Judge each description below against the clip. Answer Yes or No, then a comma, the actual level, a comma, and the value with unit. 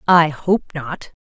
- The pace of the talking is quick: No, average, 145 wpm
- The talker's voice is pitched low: No, medium, 160 Hz